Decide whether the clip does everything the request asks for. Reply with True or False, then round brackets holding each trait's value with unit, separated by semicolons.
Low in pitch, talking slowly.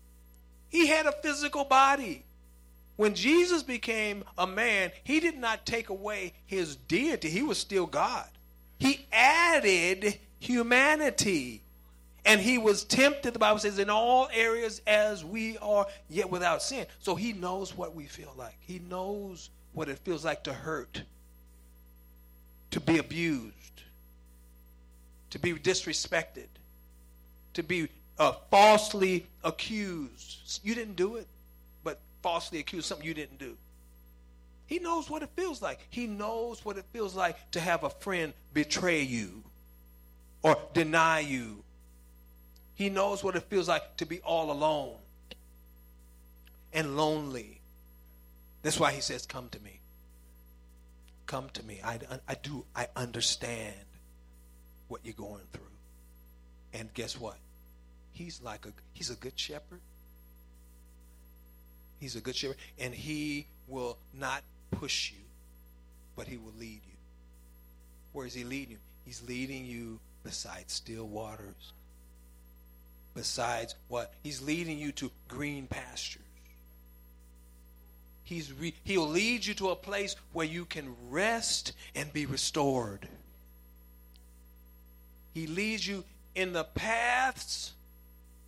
True (120 Hz; 130 wpm)